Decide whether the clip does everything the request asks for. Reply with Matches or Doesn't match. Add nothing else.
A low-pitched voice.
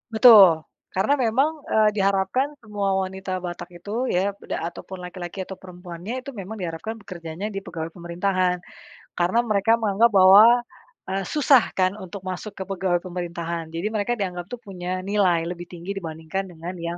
Doesn't match